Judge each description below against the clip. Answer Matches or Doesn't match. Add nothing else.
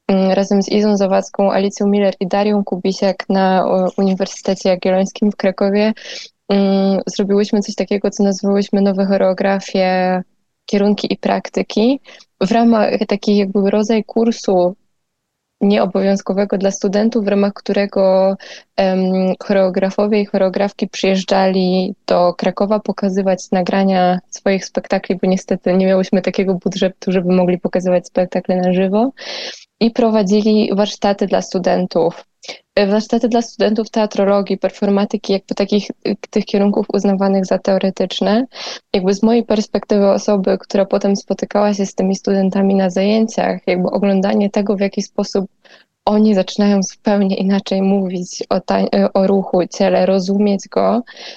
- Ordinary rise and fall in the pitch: Doesn't match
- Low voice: Doesn't match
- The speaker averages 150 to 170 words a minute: Doesn't match